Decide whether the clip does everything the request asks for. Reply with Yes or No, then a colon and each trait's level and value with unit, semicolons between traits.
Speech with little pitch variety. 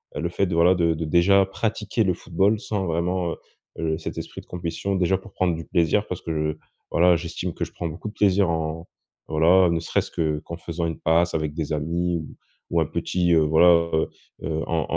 Yes: narrow, 2.1 semitones